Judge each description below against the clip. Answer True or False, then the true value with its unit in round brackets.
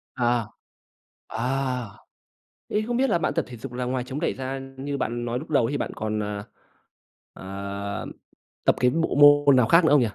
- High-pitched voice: False (130 Hz)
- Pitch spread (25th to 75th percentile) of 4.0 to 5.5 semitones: False (3.3 semitones)